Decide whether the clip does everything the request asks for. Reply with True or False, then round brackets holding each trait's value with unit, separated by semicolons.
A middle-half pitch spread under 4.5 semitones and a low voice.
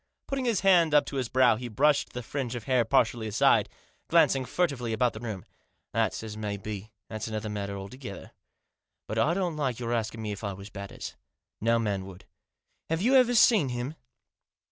False (5.1 semitones; 120 Hz)